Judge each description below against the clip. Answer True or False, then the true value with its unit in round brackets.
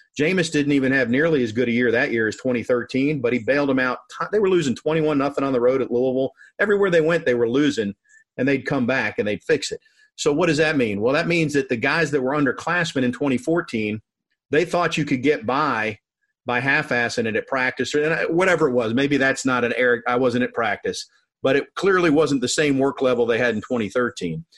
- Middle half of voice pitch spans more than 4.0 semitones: True (4.7 semitones)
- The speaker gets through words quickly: True (230 wpm)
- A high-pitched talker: False (135 Hz)